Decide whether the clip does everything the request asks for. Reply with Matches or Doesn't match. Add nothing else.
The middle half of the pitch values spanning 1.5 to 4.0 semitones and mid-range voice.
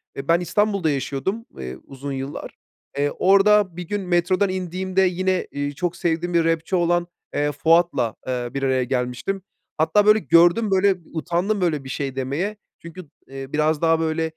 Doesn't match